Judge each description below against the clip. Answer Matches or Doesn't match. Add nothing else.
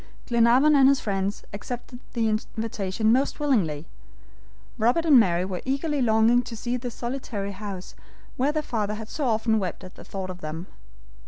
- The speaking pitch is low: Doesn't match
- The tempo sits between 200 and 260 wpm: Doesn't match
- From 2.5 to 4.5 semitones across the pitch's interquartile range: Matches